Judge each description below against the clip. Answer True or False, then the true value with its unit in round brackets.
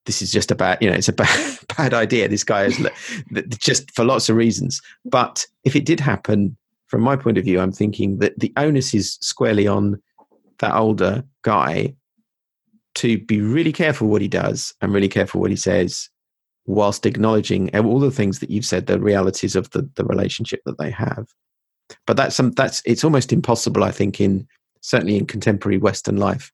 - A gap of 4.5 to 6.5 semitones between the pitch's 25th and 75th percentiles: True (5.0 semitones)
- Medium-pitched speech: False (110 Hz)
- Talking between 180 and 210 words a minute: True (190 wpm)